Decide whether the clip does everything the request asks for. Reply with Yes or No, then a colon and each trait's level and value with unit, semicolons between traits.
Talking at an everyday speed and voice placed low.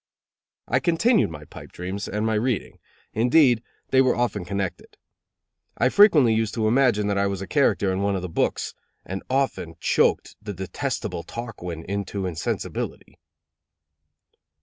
Yes: average, 150 wpm; low, 105 Hz